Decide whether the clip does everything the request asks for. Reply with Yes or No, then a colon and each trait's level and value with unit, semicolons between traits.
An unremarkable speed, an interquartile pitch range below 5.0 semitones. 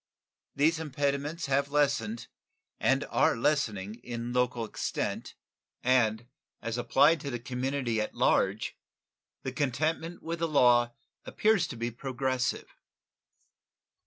No: slow, 115 wpm; average, 3.6 semitones